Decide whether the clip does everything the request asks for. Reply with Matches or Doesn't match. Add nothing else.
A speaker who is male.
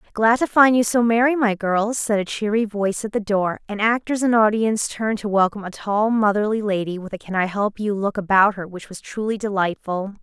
Doesn't match